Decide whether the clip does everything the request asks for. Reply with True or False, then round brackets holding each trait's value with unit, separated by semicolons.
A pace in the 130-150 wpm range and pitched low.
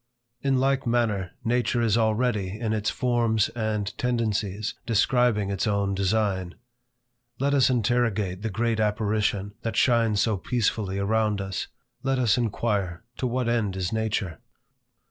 True (140 wpm; 110 Hz)